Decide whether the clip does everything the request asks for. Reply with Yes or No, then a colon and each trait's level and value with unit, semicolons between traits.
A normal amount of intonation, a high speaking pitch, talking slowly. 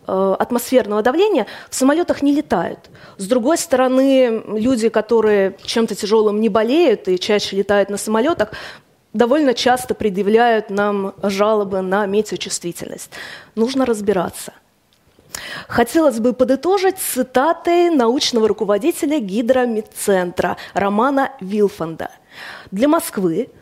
Yes: average, 4.3 semitones; high, 225 Hz; slow, 100 wpm